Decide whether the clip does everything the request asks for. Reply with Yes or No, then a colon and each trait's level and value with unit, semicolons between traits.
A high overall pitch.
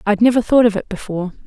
Yes: high, 215 Hz